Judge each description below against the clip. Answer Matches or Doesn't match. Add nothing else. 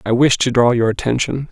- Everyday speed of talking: Doesn't match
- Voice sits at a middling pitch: Doesn't match